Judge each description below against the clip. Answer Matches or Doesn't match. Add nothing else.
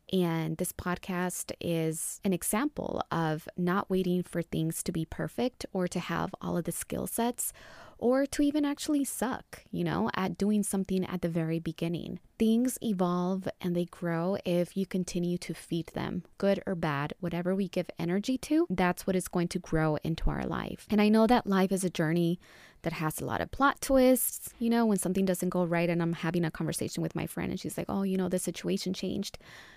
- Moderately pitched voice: Matches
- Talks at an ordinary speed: Doesn't match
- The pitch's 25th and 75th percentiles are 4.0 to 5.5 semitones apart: Doesn't match